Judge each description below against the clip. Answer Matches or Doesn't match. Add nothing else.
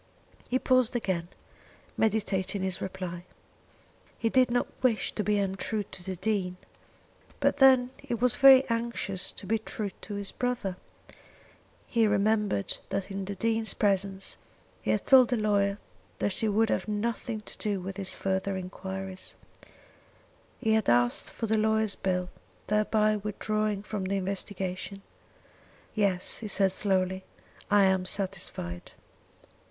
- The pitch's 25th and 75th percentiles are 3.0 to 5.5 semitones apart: Doesn't match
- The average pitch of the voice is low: Doesn't match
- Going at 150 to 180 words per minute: Doesn't match